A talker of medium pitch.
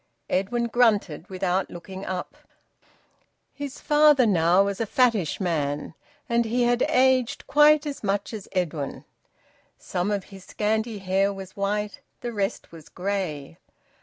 No: high, 200 Hz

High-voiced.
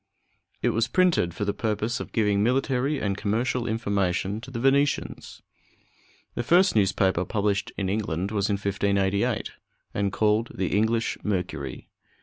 No: low, 105 Hz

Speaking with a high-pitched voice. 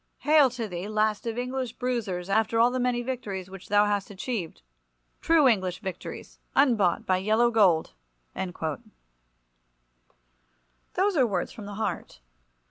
Yes: high, 200 Hz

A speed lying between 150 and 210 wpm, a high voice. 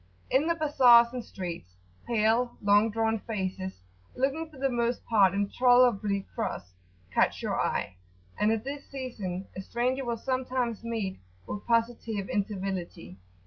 No: average, 140 wpm; high, 225 Hz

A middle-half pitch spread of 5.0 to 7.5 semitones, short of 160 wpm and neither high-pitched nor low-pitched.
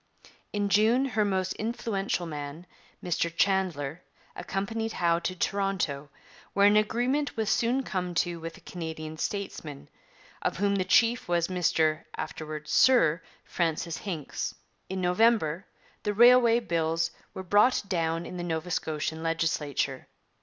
No: average, 4.3 semitones; slow, 135 wpm; medium, 180 Hz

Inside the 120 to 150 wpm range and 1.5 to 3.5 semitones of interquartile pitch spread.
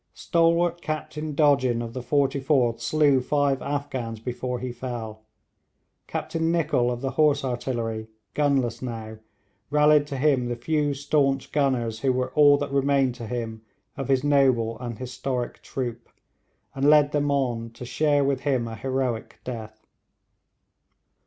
Yes: average, 145 wpm; average, 3.2 semitones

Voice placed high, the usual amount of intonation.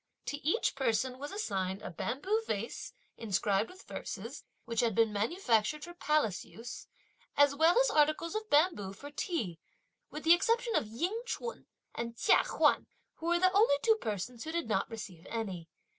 No: very high, 280 Hz; wide, 8.1 semitones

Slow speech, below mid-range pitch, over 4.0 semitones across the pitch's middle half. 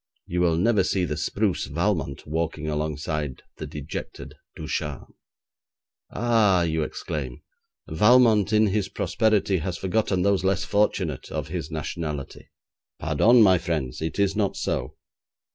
Yes: slow, 130 wpm; very low, 90 Hz; average, 5.0 semitones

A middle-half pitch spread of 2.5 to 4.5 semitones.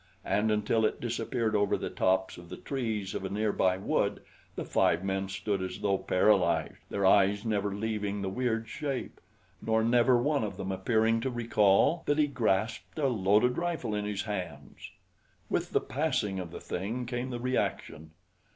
Yes: average, 3.7 semitones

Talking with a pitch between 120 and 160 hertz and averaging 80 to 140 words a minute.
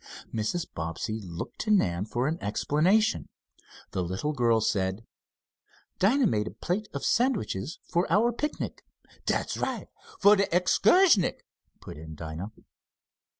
Yes: medium, 140 Hz; slow, 135 wpm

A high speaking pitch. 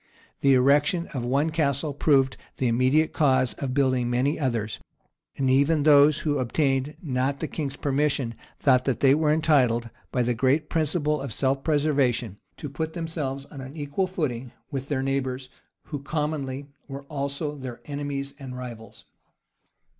No: medium, 140 Hz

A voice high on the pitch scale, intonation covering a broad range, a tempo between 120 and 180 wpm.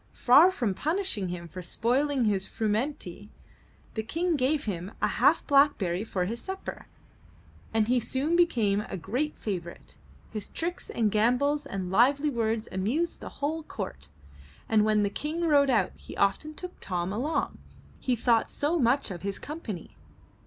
Yes: high, 235 Hz; wide, 6.7 semitones; average, 160 wpm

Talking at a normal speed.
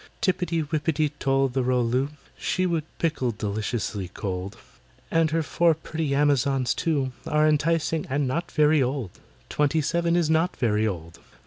Yes: average, 150 wpm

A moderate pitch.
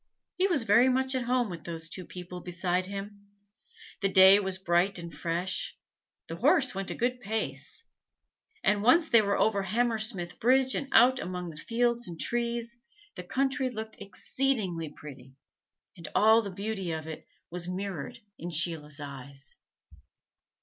No: high, 200 Hz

